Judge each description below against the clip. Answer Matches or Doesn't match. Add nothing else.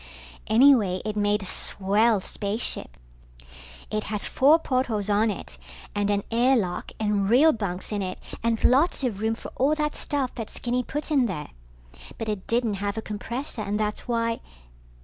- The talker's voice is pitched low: Doesn't match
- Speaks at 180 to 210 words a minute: Doesn't match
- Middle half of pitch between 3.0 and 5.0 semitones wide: Matches